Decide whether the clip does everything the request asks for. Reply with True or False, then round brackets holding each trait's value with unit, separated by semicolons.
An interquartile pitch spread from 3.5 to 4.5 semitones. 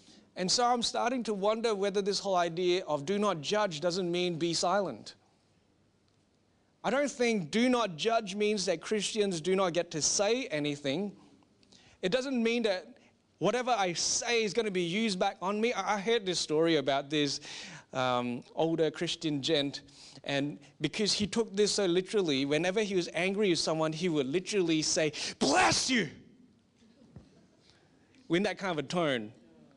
False (5.1 semitones)